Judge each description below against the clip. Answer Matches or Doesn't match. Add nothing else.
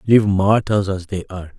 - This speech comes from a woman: Doesn't match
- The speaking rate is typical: Matches